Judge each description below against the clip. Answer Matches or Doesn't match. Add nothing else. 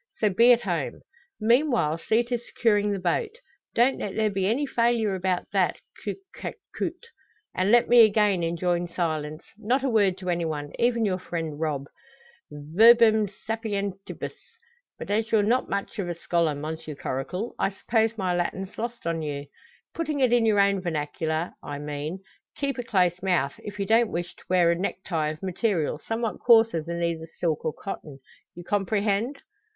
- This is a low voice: Doesn't match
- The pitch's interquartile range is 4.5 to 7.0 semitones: Matches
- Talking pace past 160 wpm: Matches